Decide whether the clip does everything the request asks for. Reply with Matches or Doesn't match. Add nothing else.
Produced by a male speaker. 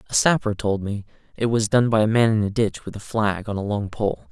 Matches